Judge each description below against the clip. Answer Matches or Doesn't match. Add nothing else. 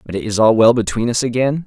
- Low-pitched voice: Matches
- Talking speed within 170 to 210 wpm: Doesn't match